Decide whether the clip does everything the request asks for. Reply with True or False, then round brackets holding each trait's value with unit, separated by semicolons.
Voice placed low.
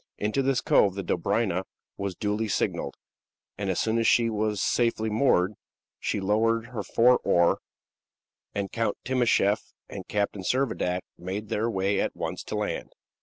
True (105 Hz)